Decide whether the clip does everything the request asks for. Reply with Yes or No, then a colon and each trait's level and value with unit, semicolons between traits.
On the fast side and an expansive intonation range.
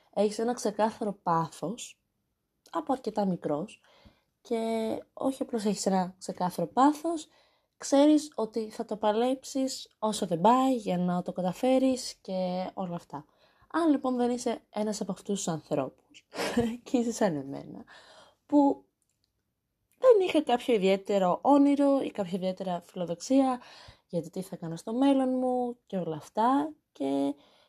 No: average, 135 wpm; wide, 6.0 semitones